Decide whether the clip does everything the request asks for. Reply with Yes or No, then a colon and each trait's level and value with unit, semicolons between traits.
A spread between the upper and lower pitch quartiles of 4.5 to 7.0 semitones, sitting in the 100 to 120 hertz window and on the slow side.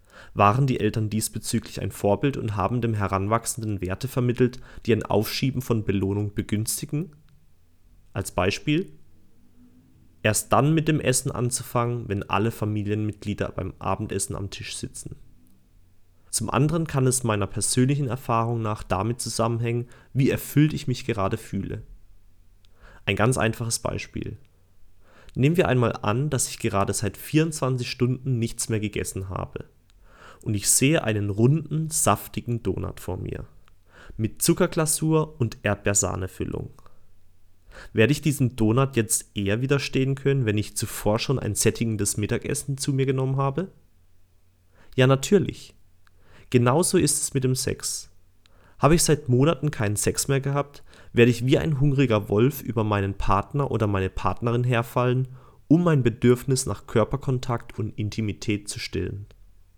No: average, 4.8 semitones; low, 115 Hz; average, 140 wpm